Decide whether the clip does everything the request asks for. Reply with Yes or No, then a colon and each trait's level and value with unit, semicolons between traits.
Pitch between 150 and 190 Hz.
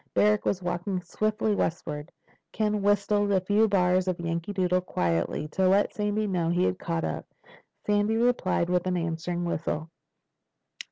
Yes: medium, 185 Hz